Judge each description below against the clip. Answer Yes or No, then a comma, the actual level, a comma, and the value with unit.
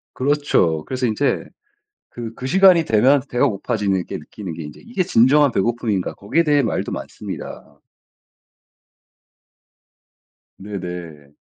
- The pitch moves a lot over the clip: Yes, wide, 7.3 semitones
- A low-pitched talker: Yes, low, 115 Hz